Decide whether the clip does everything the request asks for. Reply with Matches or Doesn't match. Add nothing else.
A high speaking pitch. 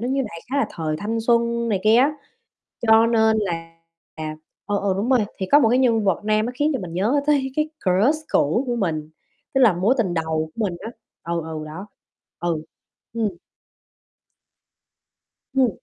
Matches